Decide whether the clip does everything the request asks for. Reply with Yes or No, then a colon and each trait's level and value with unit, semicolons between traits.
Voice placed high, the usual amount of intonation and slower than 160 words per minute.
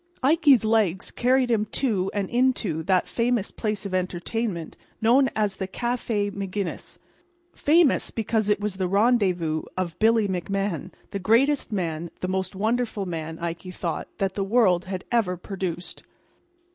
Yes: high, 200 Hz; average, 4.2 semitones; average, 145 wpm